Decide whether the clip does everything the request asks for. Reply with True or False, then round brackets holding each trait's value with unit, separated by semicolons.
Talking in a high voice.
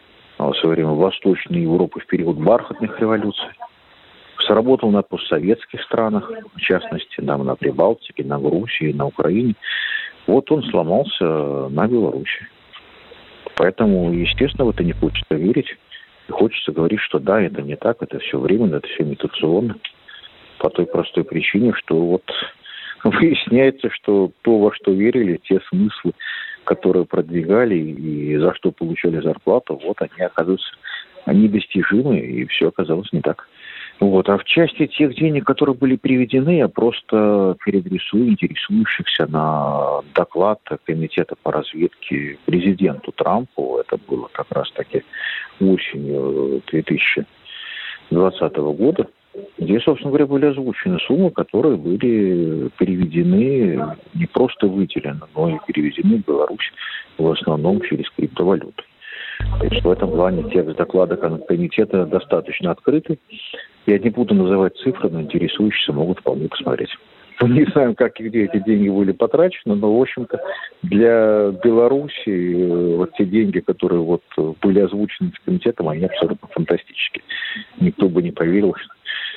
False (105 Hz)